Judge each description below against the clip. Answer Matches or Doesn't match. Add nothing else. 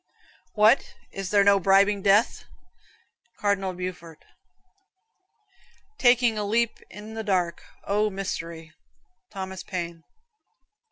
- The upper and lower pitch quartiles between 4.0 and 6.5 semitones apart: Doesn't match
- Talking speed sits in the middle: Doesn't match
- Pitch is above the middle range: Matches